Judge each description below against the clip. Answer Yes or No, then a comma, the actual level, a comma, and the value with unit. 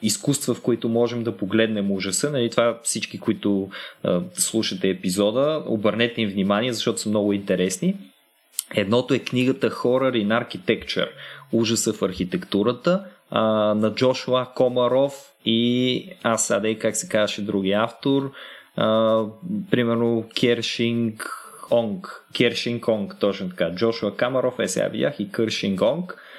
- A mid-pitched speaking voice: No, low, 115 Hz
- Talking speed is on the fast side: No, average, 130 wpm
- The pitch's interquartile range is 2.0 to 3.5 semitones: Yes, average, 2.9 semitones